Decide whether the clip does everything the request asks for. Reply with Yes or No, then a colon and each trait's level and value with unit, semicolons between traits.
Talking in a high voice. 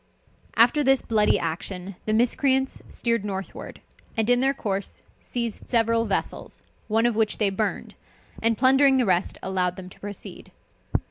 Yes: high, 225 Hz